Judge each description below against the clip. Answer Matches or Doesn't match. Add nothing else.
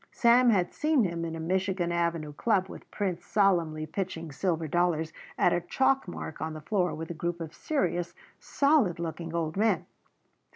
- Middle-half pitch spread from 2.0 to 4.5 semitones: Matches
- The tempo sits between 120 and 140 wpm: Doesn't match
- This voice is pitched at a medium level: Matches